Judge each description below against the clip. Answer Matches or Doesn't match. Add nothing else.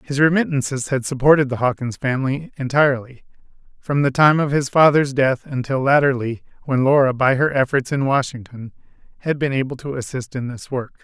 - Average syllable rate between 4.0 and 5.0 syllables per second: Doesn't match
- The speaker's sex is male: Matches